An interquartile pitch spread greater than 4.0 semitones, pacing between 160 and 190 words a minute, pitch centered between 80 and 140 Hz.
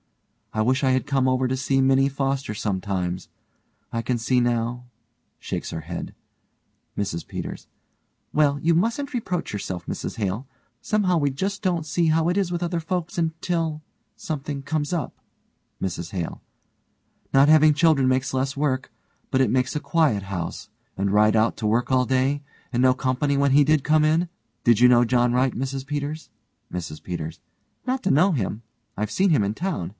Yes: average, 5.3 semitones; average, 180 wpm; low, 135 Hz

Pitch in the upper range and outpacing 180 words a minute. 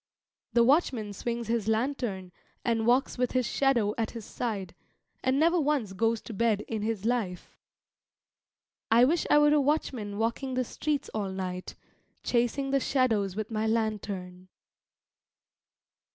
No: high, 230 Hz; average, 145 wpm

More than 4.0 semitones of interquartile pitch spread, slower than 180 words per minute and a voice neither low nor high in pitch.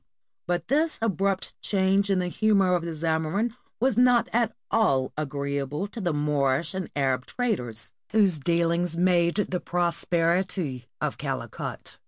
Yes: average, 4.7 semitones; average, 140 wpm; medium, 175 Hz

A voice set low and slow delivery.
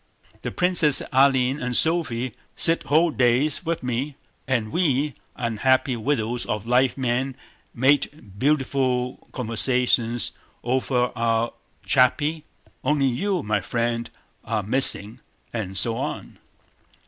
Yes: low, 125 Hz; slow, 110 wpm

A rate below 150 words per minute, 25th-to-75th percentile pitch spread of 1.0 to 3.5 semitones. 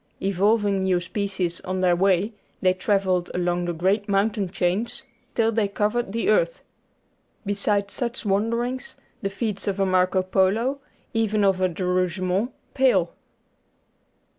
Yes: average, 140 wpm; average, 2.8 semitones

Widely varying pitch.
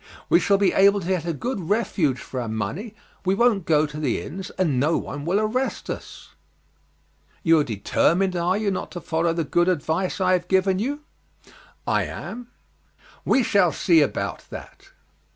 No: average, 4.0 semitones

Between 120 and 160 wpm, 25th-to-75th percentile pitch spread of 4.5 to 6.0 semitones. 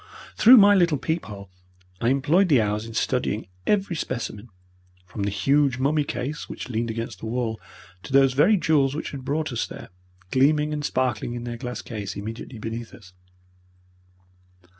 No: average, 170 wpm; average, 4.8 semitones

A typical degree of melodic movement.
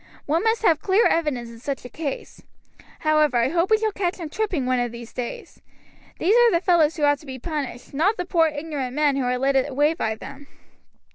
Yes: average, 4.7 semitones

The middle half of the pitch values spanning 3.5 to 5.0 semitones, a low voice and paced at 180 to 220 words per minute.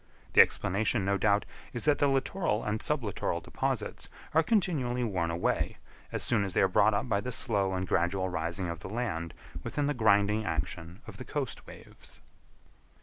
Yes: average, 4.7 semitones; low, 105 Hz; average, 185 wpm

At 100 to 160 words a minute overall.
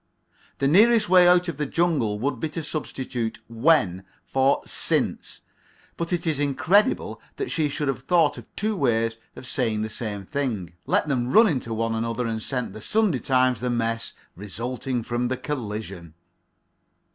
No: average, 170 wpm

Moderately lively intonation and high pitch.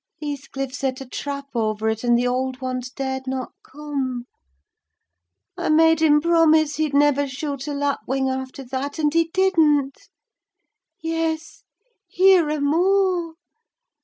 Yes: average, 3.4 semitones; very high, 285 Hz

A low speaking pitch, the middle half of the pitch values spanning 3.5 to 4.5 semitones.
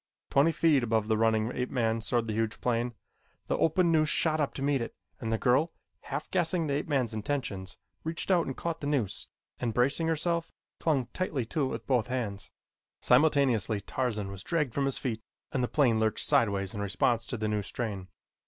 No: low, 125 Hz; average, 5.2 semitones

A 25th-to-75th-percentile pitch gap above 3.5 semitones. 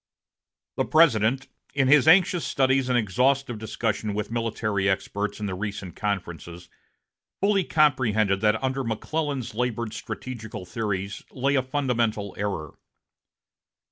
Yes: average, 4.6 semitones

